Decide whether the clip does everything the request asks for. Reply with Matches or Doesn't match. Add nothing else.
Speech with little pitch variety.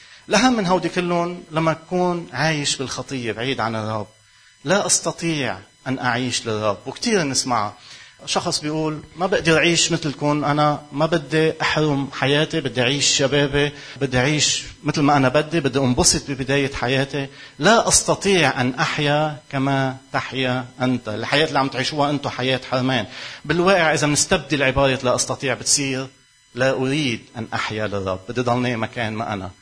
Doesn't match